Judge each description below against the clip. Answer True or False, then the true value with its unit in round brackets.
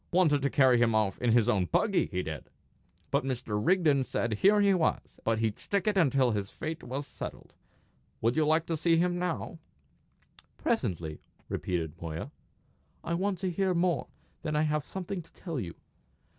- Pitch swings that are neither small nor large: False (8.0 semitones)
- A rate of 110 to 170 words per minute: False (185 wpm)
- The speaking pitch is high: False (145 Hz)